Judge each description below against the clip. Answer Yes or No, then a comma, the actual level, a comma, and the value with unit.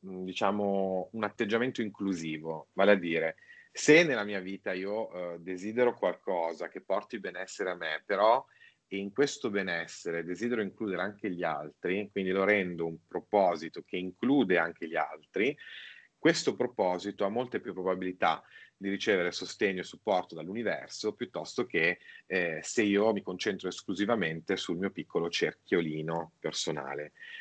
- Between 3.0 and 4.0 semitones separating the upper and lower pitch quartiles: No, narrow, 2.6 semitones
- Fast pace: No, average, 140 wpm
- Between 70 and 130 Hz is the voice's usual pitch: Yes, very low, 95 Hz